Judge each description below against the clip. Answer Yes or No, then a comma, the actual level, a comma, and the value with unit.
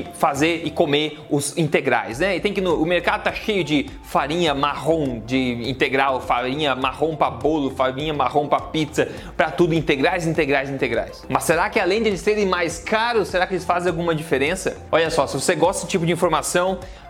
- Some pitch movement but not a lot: Yes, average, 3.8 semitones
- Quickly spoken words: Yes, fast, 195 wpm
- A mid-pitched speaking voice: Yes, medium, 160 Hz